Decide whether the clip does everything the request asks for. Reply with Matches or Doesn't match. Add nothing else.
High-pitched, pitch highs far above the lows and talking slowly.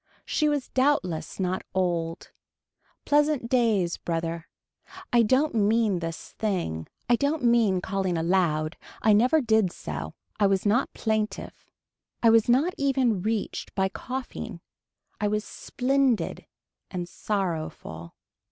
Matches